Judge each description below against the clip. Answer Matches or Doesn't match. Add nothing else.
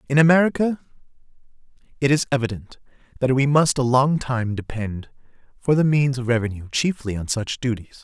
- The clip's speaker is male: Matches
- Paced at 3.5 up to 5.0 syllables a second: Doesn't match